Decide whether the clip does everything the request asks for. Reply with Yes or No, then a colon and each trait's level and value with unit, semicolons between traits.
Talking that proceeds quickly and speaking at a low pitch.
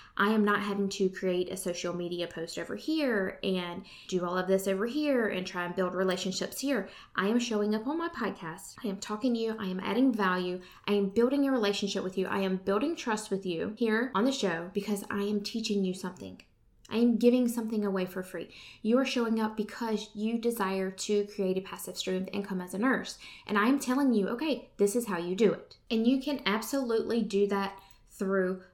No: fast, 225 wpm; high, 205 Hz